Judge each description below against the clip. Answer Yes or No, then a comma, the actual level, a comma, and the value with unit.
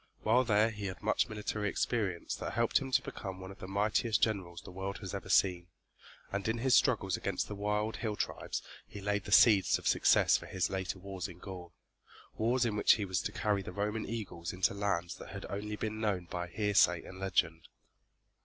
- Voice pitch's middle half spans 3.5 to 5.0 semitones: No, narrow, 2.4 semitones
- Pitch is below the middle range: Yes, low, 100 Hz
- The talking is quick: Yes, fast, 210 wpm